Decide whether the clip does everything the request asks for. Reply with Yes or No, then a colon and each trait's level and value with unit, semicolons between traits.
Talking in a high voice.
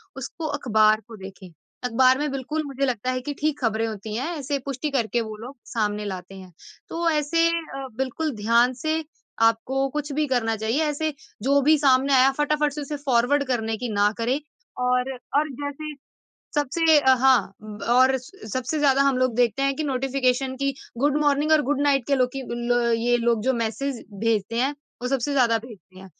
Yes: very high, 260 Hz